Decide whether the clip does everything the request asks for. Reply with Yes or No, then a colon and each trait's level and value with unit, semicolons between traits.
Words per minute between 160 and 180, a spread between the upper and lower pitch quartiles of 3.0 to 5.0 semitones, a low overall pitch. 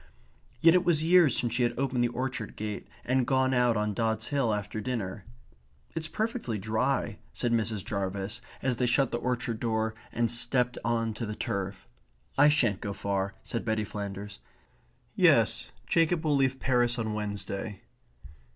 Yes: average, 170 wpm; average, 3.7 semitones; low, 115 Hz